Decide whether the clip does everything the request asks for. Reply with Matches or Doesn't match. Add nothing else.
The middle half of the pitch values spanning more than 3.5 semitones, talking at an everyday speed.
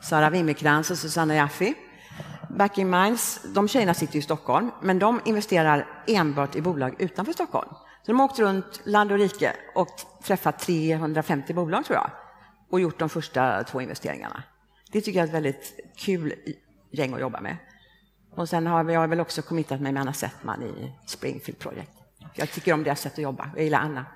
Matches